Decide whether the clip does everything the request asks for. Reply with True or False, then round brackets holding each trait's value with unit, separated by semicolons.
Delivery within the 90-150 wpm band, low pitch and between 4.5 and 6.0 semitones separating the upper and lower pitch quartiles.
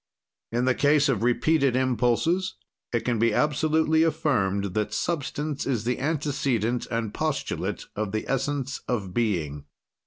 True (135 wpm; 125 Hz; 5.2 semitones)